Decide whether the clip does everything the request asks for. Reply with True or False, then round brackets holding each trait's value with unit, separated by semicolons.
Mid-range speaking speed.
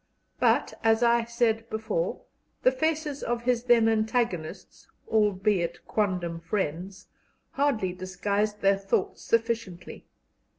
False (110 wpm)